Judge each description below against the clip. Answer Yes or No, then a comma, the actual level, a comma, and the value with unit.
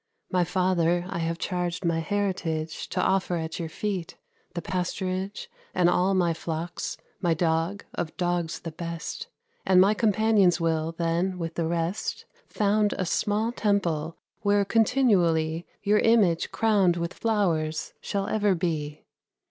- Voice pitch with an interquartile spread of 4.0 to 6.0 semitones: No, average, 3.4 semitones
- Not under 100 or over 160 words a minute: Yes, average, 140 wpm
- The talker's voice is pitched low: No, medium, 180 Hz